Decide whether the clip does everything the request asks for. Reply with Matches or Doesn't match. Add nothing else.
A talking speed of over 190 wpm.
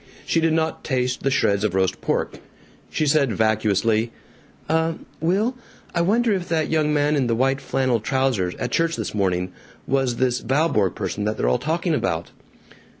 Doesn't match